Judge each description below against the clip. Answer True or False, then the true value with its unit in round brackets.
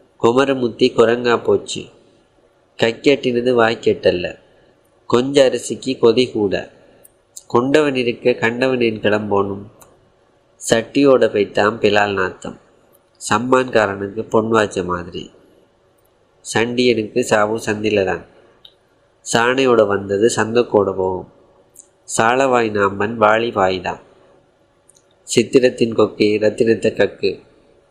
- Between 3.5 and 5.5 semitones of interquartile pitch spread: False (3.1 semitones)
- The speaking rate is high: False (85 wpm)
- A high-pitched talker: False (115 Hz)